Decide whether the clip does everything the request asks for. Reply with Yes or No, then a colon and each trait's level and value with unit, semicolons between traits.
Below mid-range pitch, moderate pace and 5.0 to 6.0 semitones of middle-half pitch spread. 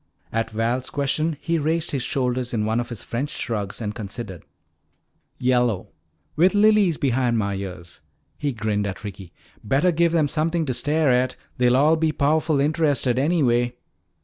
Yes: low, 130 Hz; average, 160 wpm; wide, 5.4 semitones